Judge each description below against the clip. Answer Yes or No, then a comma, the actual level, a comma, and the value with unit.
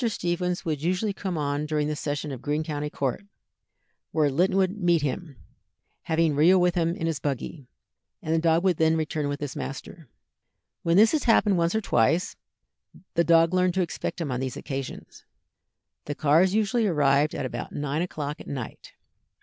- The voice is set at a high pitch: No, medium, 160 Hz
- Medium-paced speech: Yes, average, 180 wpm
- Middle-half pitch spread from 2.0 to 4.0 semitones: Yes, average, 3.6 semitones